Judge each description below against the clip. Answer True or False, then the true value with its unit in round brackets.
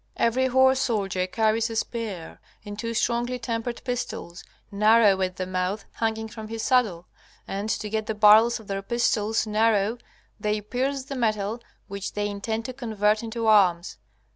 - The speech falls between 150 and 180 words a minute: True (165 wpm)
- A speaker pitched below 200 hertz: False (220 Hz)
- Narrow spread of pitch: True (2.3 semitones)